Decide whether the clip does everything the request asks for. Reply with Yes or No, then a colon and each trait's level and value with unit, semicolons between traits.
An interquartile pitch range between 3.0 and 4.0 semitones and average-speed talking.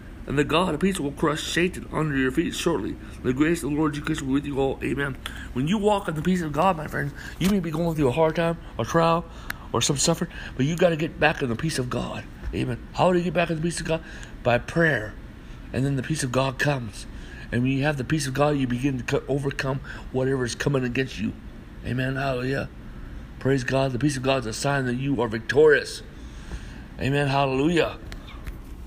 No: average, 3.7 semitones; fast, 235 wpm